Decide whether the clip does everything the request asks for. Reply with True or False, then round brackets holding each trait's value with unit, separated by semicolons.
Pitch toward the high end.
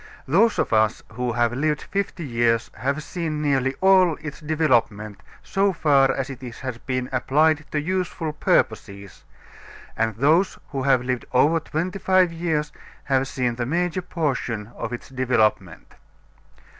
False (140 Hz)